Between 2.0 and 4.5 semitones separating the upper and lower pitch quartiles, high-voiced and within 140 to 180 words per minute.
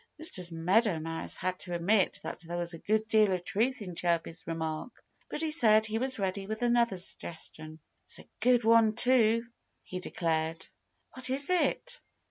No: wide, 5.6 semitones; high, 205 Hz; average, 175 wpm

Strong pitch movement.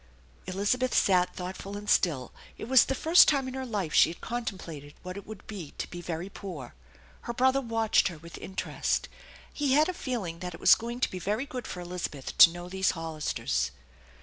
Yes: wide, 5.8 semitones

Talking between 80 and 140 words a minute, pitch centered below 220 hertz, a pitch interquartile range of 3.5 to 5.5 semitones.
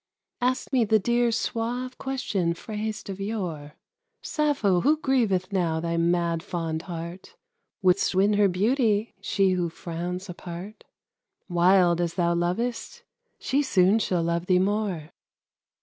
Yes: slow, 135 wpm; high, 190 Hz; average, 4.6 semitones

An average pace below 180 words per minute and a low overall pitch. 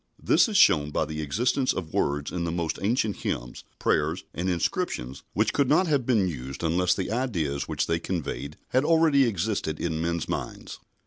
No: average, 185 wpm; very low, 85 Hz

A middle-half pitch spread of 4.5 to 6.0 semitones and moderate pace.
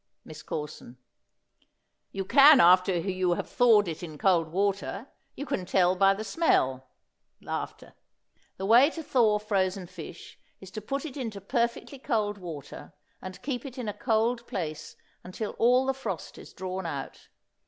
Yes: average, 5.1 semitones; average, 160 wpm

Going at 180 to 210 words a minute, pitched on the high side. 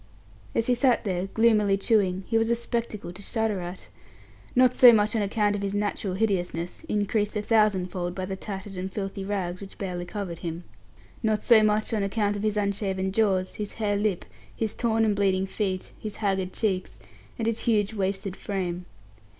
Yes: average, 190 wpm; high, 205 Hz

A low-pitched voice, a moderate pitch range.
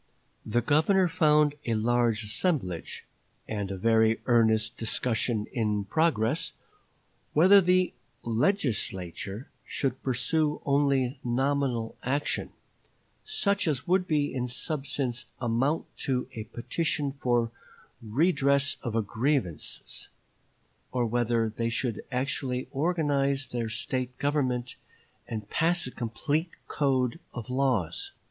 Yes: low, 125 Hz; average, 4.2 semitones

